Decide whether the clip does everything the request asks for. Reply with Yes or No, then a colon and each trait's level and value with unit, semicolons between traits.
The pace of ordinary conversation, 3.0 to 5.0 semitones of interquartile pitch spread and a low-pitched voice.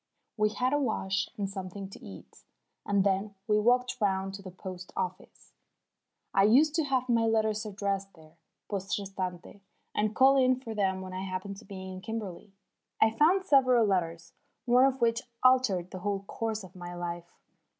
No: average, 180 wpm; average, 3.6 semitones; high, 200 Hz